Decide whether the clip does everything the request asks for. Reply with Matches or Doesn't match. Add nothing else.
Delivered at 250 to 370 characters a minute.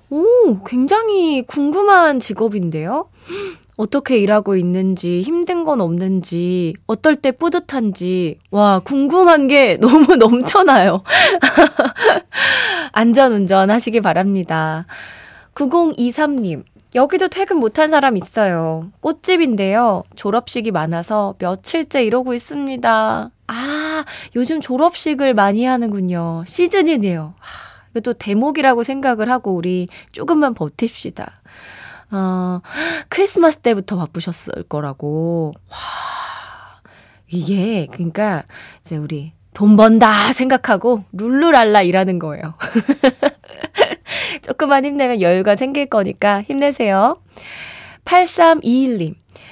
Doesn't match